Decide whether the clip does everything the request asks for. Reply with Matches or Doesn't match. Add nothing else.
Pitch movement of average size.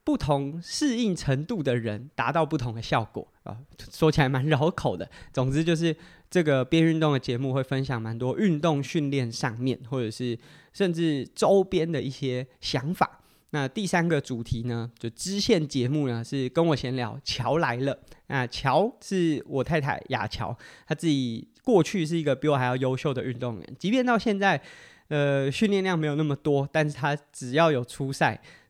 Matches